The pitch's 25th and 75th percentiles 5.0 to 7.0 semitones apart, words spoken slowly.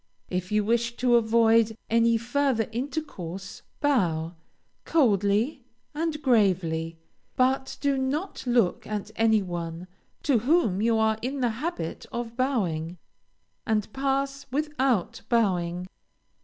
Yes: wide, 5.4 semitones; slow, 115 wpm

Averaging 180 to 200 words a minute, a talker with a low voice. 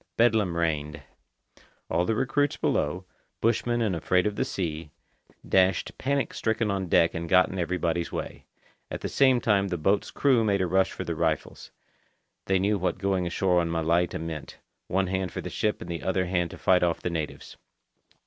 Yes: average, 185 wpm; very low, 95 Hz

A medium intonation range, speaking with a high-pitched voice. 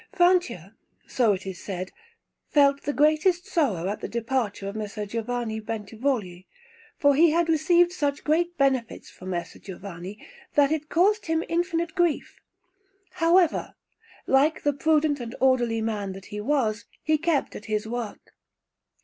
No: wide, 7.0 semitones; very high, 265 Hz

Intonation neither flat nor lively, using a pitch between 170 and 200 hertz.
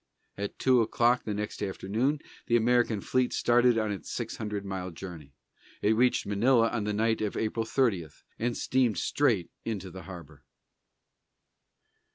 No: average, 3.7 semitones; low, 110 Hz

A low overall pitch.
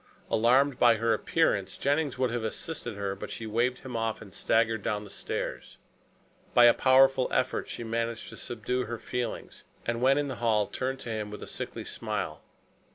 Yes: low, 120 Hz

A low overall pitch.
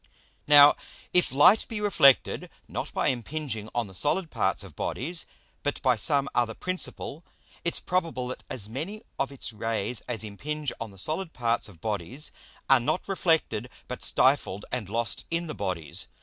Yes: low, 130 Hz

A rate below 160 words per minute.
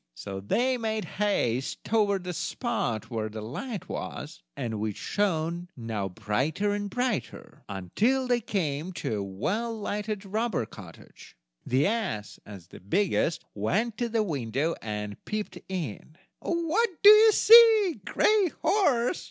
Yes: average, 140 wpm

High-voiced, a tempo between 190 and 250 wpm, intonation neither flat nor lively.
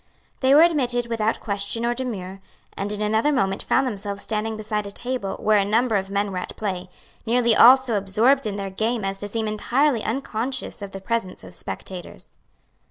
Yes: high, 215 Hz; average, 195 wpm; average, 3.4 semitones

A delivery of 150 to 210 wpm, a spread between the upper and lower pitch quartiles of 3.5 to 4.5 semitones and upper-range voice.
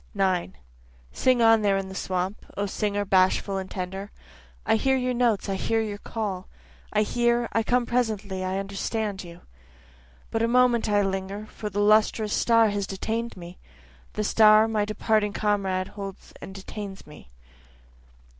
No: average, 160 wpm; narrow, 2.5 semitones; high, 205 Hz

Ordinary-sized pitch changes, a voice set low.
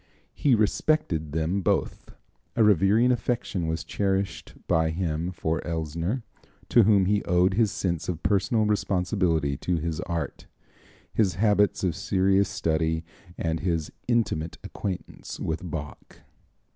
Yes: average, 4.0 semitones; very low, 90 Hz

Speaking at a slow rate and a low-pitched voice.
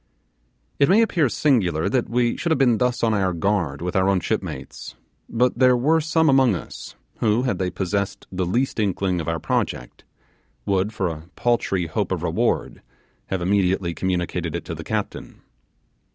No: average, 175 wpm; low, 100 Hz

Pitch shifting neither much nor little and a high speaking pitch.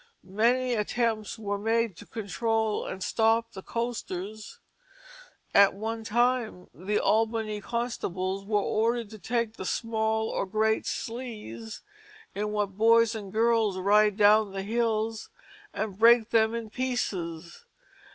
No: narrow, 2.1 semitones; high, 220 Hz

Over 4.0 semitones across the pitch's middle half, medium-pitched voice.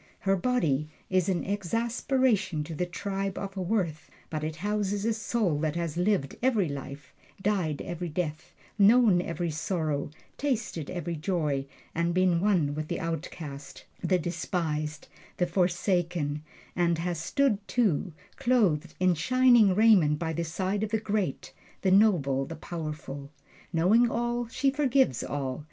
Yes: average, 5.1 semitones; medium, 180 Hz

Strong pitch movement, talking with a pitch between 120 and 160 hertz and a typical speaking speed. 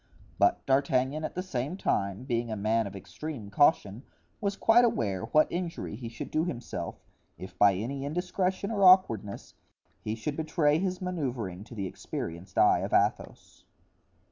Yes: wide, 8.9 semitones; low, 135 Hz; average, 160 wpm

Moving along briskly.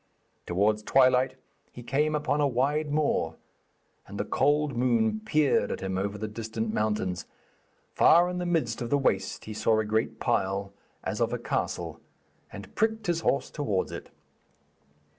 No: average, 160 wpm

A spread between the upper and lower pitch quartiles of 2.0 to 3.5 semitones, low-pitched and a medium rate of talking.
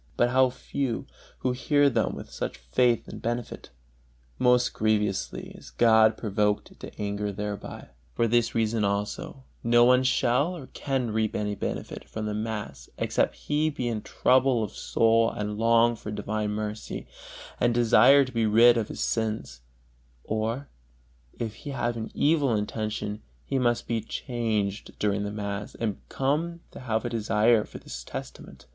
Yes: average, 2.8 semitones; low, 115 Hz; average, 160 wpm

